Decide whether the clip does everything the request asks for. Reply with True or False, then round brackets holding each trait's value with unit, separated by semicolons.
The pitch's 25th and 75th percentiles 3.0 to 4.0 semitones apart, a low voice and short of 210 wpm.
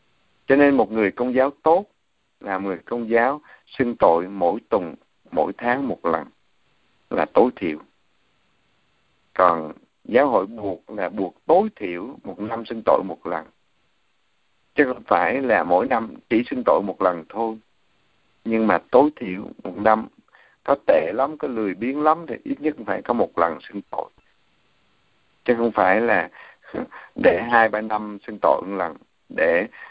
True (3.7 semitones; 110 Hz; 165 wpm)